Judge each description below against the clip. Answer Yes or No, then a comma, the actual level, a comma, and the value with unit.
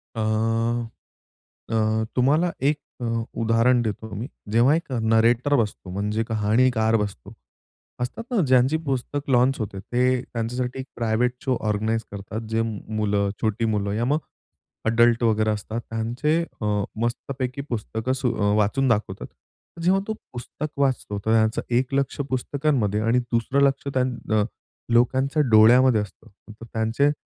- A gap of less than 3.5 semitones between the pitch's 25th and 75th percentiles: Yes, average, 2.9 semitones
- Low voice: Yes, low, 115 Hz